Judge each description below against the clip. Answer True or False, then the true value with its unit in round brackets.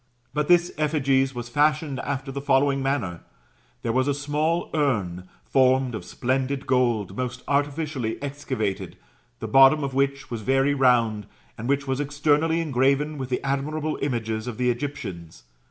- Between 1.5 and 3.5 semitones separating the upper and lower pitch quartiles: True (2.9 semitones)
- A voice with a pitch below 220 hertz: True (135 Hz)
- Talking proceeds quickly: False (155 wpm)